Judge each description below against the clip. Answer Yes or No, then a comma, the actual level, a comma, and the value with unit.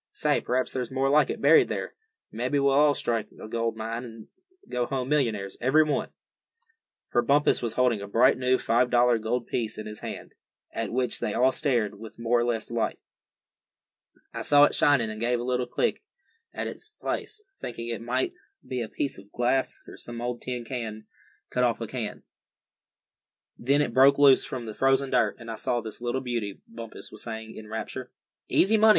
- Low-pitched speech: Yes, low, 120 Hz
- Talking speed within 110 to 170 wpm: No, average, 195 wpm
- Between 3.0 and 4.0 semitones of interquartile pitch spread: No, narrow, 2.6 semitones